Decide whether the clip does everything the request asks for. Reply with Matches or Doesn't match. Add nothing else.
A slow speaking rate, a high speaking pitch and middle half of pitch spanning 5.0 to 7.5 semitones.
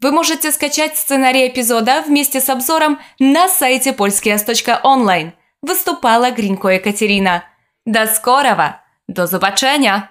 Matches